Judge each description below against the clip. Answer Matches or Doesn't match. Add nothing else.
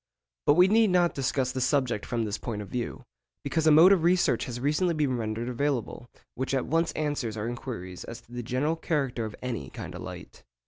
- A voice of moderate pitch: Doesn't match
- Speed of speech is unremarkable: Doesn't match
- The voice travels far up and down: Doesn't match